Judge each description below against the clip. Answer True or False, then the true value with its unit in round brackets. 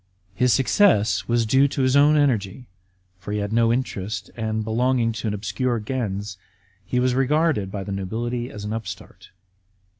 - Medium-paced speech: True (170 wpm)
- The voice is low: True (115 Hz)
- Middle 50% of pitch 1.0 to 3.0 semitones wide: False (3.8 semitones)